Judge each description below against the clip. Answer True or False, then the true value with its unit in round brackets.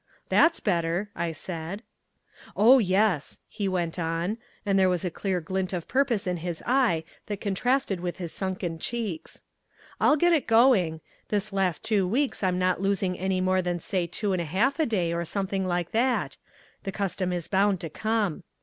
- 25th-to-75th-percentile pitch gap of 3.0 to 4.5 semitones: True (3.4 semitones)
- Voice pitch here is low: False (190 Hz)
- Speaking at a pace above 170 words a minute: True (180 wpm)